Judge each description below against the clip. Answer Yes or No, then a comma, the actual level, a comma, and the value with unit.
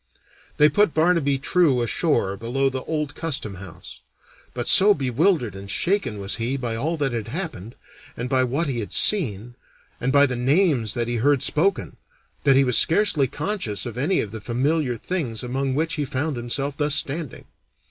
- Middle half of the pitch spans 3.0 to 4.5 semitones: No, average, 4.9 semitones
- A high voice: No, low, 135 Hz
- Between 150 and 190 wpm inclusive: Yes, average, 180 wpm